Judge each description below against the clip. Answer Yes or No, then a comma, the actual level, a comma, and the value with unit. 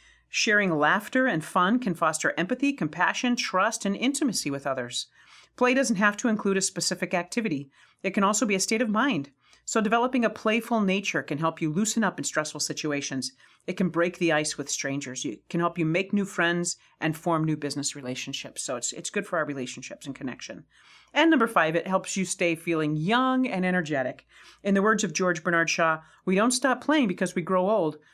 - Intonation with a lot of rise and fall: Yes, wide, 5.8 semitones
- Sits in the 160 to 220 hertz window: Yes, medium, 185 Hz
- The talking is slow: No, fast, 205 wpm